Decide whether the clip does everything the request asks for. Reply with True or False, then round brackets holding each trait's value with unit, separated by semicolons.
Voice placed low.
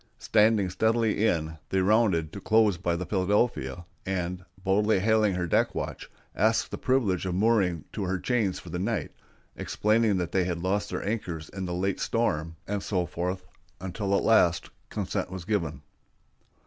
True (95 Hz)